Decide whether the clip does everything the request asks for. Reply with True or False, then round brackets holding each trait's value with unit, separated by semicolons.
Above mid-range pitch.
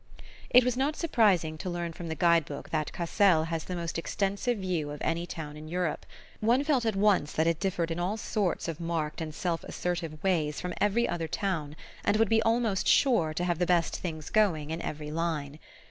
False (175 Hz)